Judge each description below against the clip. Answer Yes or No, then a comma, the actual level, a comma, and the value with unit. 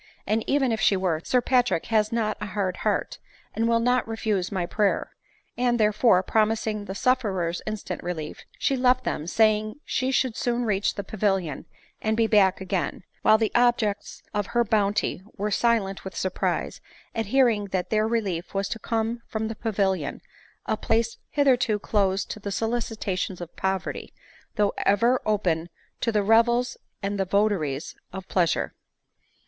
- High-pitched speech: Yes, high, 215 Hz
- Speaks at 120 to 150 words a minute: No, average, 165 wpm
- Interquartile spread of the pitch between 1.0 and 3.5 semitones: Yes, average, 3.1 semitones